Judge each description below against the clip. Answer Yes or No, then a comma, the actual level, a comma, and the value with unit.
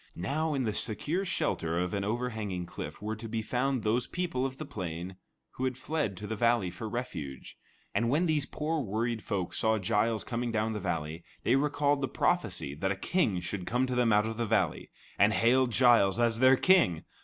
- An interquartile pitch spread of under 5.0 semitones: Yes, average, 4.5 semitones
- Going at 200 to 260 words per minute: Yes, fast, 205 wpm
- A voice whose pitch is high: No, low, 115 Hz